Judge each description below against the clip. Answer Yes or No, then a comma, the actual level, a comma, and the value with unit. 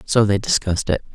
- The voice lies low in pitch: Yes, low, 105 Hz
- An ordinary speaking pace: No, fast, 210 wpm